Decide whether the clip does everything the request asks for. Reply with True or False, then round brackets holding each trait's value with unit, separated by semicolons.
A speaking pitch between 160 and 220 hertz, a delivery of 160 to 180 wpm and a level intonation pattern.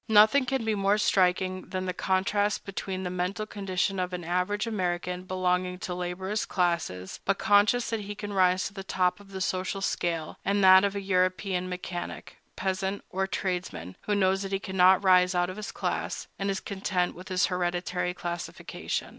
False (185 Hz; 190 wpm; 1.6 semitones)